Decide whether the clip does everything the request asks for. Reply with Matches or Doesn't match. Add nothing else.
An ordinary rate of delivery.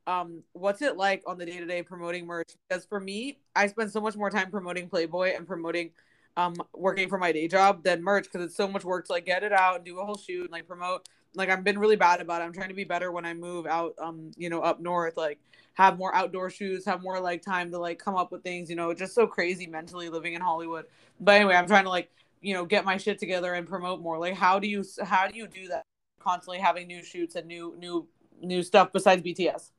Doesn't match